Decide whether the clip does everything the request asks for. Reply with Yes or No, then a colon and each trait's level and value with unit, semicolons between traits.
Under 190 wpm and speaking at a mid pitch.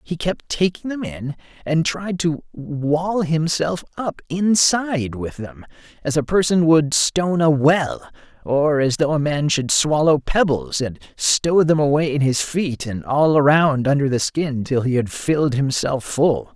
Yes: average, 175 wpm; medium, 150 Hz